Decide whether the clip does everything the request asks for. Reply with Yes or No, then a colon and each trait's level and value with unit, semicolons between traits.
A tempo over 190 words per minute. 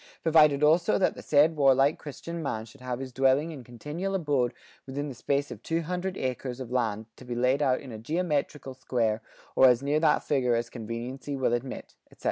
Yes: fast, 205 wpm